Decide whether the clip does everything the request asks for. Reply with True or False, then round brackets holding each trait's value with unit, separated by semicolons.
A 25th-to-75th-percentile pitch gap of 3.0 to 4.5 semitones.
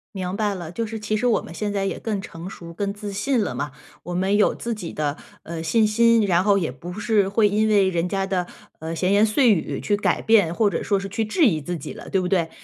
True (3.4 semitones)